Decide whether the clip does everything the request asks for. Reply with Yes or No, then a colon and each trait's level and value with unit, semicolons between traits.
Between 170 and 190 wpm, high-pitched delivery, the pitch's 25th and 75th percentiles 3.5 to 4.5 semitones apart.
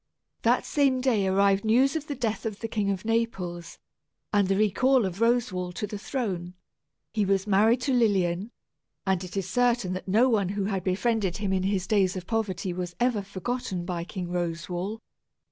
Yes: average, 185 wpm; high, 200 Hz; average, 3.8 semitones